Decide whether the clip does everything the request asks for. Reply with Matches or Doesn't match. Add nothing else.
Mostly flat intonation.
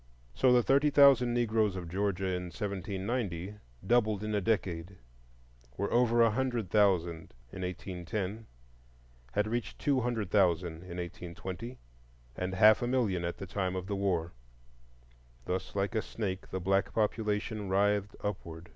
Doesn't match